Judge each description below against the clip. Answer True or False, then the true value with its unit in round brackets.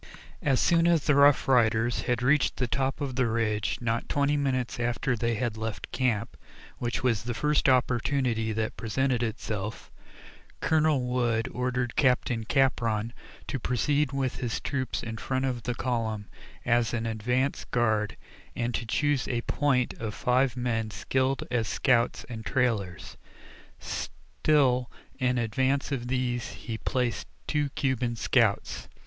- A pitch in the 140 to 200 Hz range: False (125 Hz)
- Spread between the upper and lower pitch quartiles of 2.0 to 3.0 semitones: True (2.5 semitones)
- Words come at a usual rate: True (145 wpm)